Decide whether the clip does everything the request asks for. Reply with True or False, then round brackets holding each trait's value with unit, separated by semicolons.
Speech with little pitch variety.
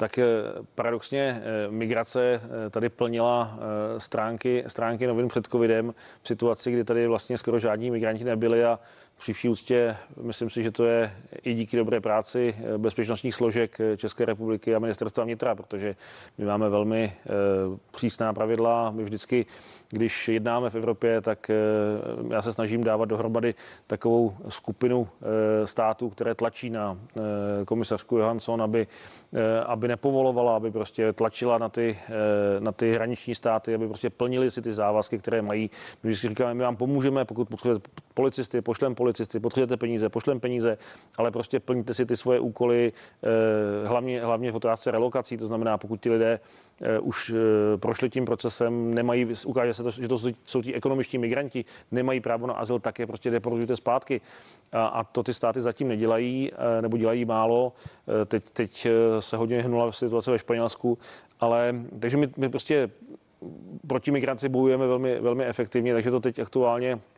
True (1.6 semitones)